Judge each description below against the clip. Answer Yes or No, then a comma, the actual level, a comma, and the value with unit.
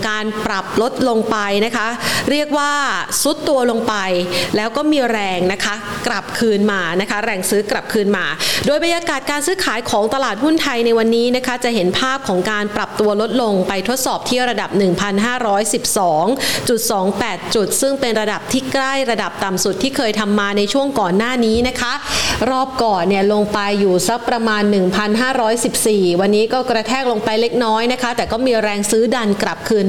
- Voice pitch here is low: No, high, 225 Hz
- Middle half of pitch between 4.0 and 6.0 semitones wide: No, average, 3.5 semitones